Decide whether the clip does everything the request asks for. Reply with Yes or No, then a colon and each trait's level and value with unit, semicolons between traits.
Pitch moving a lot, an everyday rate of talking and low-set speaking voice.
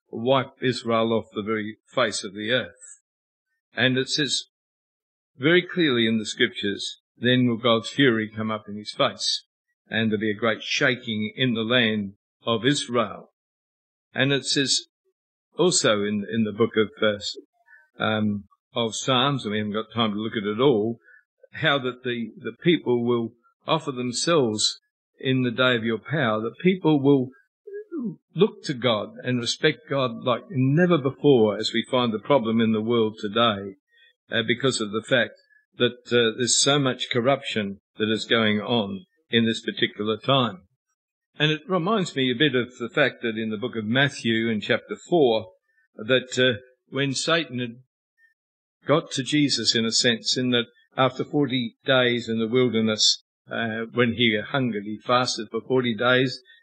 No: average, 4.3 semitones; average, 170 wpm; low, 125 Hz